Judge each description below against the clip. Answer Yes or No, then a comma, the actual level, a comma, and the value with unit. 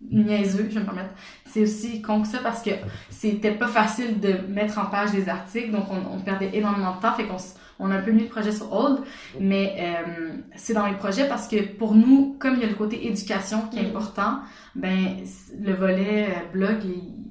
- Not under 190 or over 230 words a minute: Yes, fast, 220 wpm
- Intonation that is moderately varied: No, narrow, 2.1 semitones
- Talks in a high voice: Yes, high, 210 Hz